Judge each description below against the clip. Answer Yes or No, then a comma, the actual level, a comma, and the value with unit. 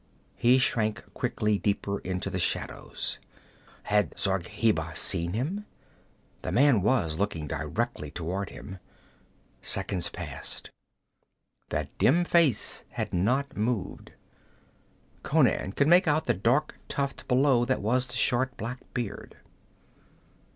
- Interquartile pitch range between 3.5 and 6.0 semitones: Yes, wide, 5.5 semitones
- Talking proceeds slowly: Yes, slow, 115 wpm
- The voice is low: Yes, low, 110 Hz